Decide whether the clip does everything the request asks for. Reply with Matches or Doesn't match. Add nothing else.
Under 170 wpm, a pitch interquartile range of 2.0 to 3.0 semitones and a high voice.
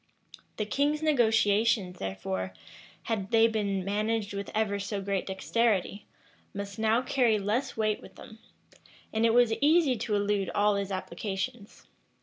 Matches